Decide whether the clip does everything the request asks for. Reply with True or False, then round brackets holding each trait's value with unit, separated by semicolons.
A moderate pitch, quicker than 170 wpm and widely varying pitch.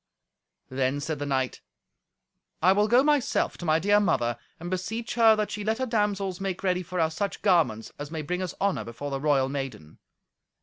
True (180 Hz; 200 wpm; 6.4 semitones)